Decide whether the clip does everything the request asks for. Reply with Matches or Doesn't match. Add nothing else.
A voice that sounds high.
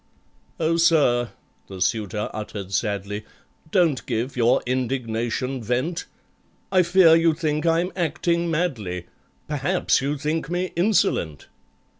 Doesn't match